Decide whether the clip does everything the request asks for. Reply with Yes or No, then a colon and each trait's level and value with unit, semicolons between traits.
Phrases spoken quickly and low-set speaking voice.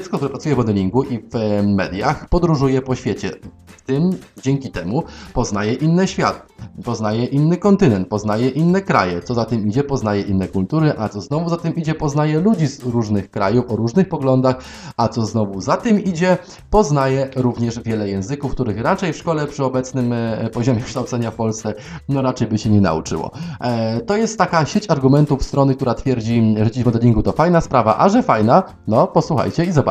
Yes: fast, 190 wpm; low, 130 Hz